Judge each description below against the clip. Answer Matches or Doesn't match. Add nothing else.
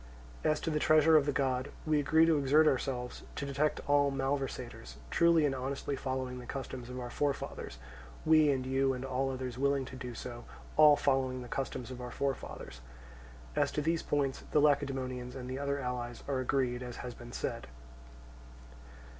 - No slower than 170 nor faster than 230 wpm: Matches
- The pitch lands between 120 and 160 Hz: Matches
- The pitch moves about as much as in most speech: Doesn't match